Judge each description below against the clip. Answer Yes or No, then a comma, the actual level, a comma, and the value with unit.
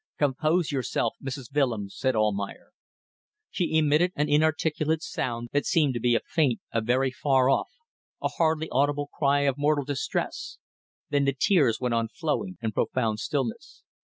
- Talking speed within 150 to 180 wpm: Yes, average, 160 wpm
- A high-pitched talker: No, medium, 140 Hz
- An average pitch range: Yes, average, 3.8 semitones